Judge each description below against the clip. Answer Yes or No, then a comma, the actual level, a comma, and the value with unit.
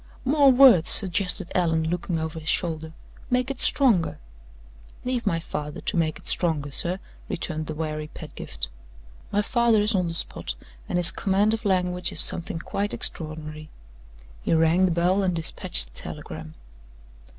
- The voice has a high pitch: No, medium, 175 Hz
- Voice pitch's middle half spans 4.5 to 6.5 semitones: No, average, 4.1 semitones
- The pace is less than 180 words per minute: Yes, average, 160 wpm